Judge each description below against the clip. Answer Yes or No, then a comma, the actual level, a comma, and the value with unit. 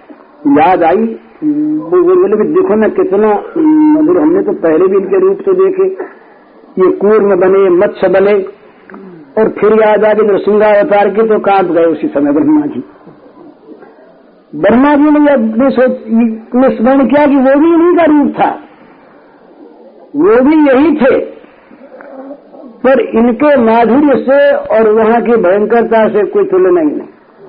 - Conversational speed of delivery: Yes, average, 150 wpm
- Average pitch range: No, wide, 6.2 semitones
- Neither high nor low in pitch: No, very high, 270 Hz